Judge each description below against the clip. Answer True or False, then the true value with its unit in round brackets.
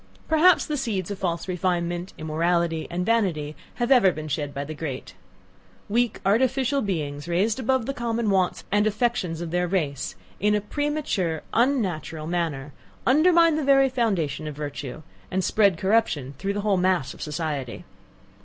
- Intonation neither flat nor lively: False (6.6 semitones)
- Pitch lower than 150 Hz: False (185 Hz)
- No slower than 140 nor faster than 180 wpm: True (160 wpm)